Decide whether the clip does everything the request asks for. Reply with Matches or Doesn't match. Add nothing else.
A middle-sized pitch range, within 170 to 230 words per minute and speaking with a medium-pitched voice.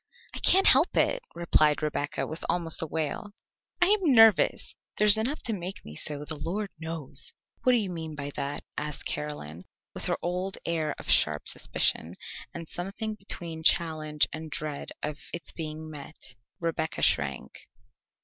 Doesn't match